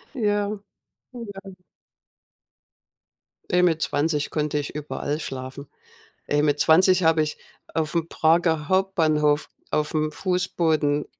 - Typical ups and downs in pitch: Yes, average, 3.2 semitones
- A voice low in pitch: No, medium, 155 Hz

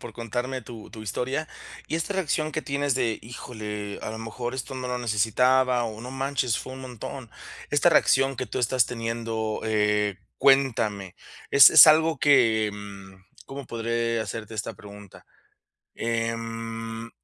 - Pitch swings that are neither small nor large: Yes, average, 3.0 semitones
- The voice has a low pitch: Yes, low, 115 Hz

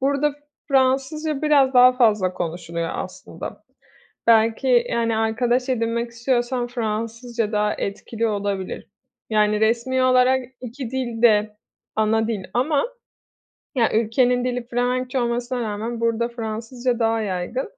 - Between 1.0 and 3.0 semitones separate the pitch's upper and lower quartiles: Yes, narrow, 2.4 semitones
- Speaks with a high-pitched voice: Yes, high, 235 Hz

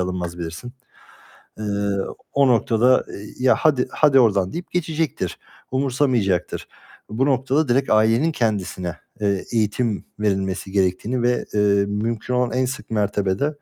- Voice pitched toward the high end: No, low, 115 Hz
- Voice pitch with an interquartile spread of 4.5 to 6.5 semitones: Yes, average, 4.8 semitones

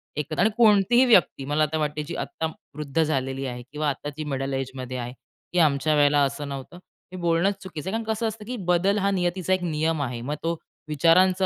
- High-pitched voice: No, medium, 155 Hz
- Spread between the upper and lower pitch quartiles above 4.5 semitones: Yes, average, 4.9 semitones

